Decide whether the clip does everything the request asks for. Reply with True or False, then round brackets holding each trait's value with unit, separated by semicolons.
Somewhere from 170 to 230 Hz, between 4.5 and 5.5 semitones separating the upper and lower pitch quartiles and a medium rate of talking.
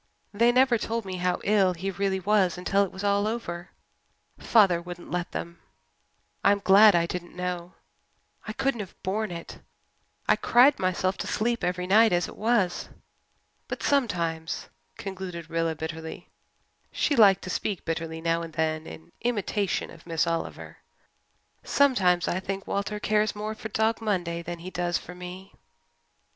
False (185 Hz; 3.6 semitones; 160 wpm)